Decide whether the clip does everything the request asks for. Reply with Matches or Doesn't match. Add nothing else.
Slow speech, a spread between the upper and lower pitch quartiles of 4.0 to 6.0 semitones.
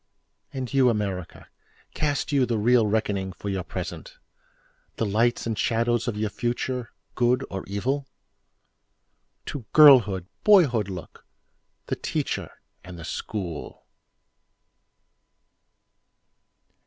Matches